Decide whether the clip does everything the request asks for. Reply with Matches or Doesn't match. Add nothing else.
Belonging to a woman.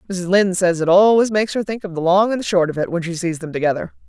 Matches